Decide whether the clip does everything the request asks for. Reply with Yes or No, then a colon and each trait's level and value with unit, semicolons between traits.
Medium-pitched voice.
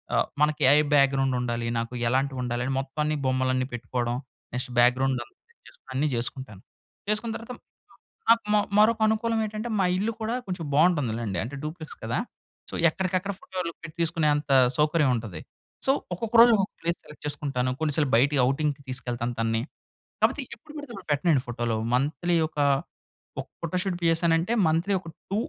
Yes: medium, 150 Hz